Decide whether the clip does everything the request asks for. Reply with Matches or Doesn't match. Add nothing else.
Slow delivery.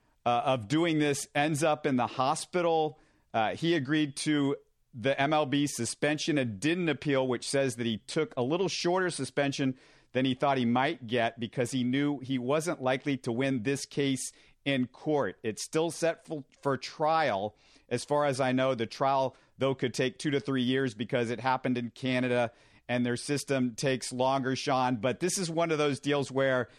Doesn't match